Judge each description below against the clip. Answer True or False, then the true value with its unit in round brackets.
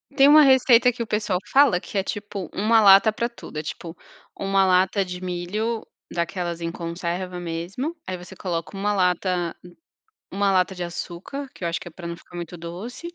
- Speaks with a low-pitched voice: False (185 Hz)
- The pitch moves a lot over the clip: False (3.5 semitones)